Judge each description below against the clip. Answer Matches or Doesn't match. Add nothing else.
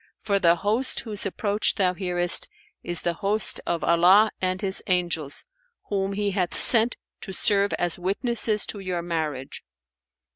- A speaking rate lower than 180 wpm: Matches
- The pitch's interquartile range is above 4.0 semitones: Doesn't match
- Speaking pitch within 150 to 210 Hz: Matches